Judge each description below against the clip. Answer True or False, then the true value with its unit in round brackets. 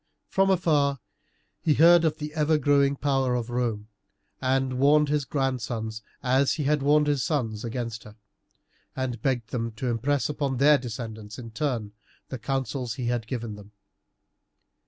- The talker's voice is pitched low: True (130 Hz)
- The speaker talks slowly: False (155 wpm)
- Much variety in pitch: False (3.7 semitones)